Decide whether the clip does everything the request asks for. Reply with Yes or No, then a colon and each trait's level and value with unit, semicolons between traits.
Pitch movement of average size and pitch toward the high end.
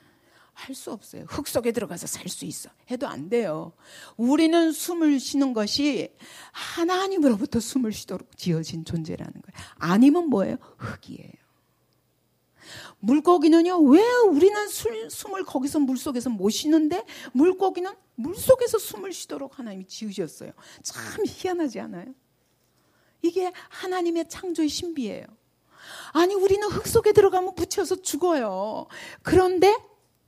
No: wide, 6.5 semitones; very high, 320 Hz